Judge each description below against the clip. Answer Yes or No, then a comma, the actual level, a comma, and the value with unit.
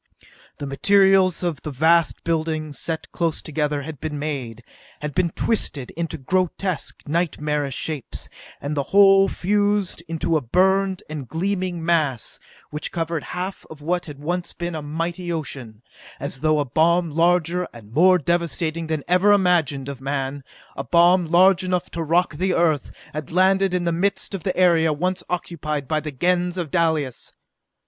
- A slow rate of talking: No, average, 165 wpm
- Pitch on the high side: No, medium, 165 Hz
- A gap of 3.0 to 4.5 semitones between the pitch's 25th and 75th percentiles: Yes, average, 3.3 semitones